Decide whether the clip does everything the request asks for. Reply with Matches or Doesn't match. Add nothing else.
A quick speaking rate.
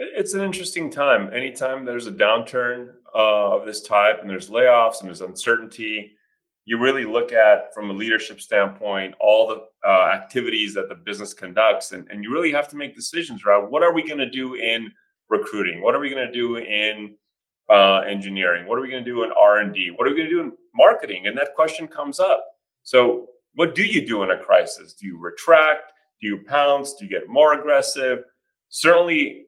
Matches